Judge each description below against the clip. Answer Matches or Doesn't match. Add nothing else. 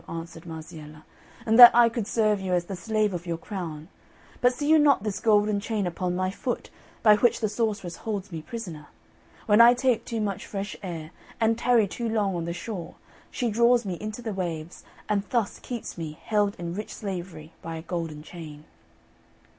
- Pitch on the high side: Matches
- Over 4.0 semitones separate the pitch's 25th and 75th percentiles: Matches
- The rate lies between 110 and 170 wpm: Doesn't match